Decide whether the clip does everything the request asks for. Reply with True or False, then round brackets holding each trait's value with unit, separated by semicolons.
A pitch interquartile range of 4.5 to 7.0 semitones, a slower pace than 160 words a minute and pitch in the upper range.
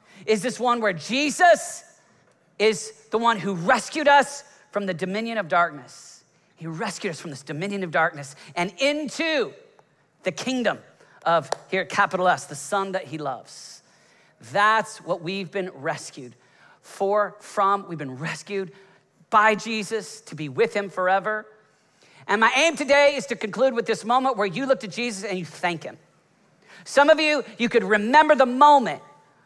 False (5.3 semitones; 165 wpm; 210 Hz)